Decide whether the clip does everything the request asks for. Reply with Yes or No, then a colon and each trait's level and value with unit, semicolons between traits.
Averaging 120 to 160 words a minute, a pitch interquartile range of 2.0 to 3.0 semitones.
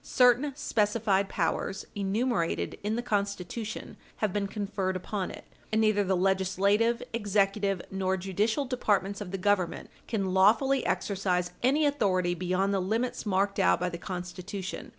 Yes: average, 145 wpm; narrow, 2.6 semitones